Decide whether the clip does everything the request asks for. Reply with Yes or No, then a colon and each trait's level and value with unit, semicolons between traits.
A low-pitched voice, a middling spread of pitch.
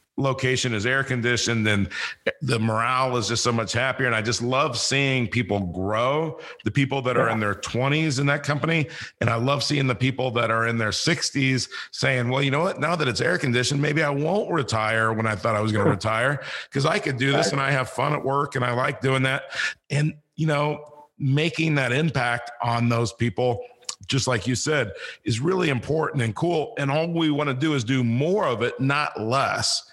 Yes: low, 130 Hz; average, 3.8 semitones